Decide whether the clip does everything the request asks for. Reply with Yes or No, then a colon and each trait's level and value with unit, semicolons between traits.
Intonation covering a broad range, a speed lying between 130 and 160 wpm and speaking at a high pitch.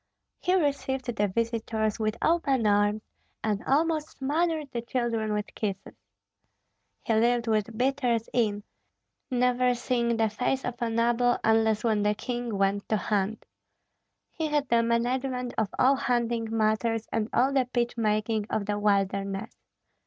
No: average, 2.7 semitones; average, 145 wpm; high, 230 Hz